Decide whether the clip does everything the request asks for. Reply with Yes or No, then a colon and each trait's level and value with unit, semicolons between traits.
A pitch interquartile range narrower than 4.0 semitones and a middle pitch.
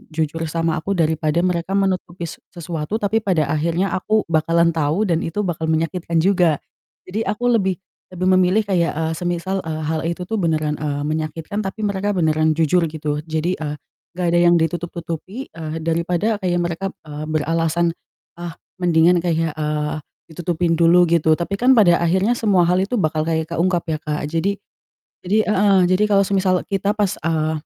Yes: average, 2.7 semitones; medium, 170 Hz